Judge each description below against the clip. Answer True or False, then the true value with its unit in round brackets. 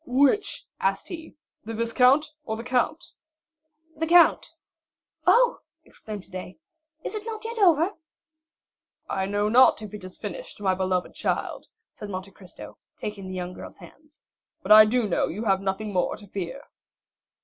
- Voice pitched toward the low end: False (215 Hz)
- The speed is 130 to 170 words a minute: True (160 wpm)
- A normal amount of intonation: False (7.9 semitones)